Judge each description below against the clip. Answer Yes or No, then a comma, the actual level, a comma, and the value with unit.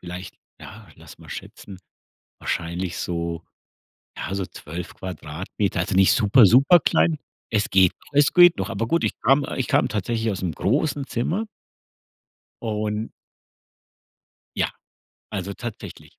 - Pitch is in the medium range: No, low, 100 Hz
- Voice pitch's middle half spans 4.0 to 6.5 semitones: Yes, average, 4.8 semitones